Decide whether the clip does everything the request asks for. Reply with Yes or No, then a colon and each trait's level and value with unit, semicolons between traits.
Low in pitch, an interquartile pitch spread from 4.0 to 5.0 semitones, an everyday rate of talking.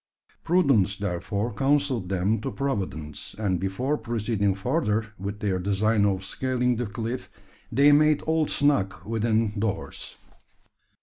No: low, 110 Hz; average, 4.7 semitones; slow, 125 wpm